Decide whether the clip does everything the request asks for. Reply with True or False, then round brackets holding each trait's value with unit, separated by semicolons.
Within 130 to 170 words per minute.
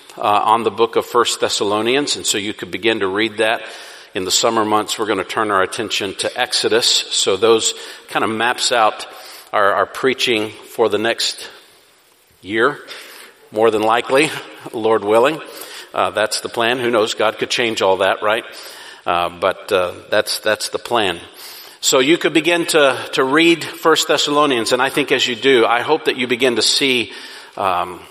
False (185 wpm)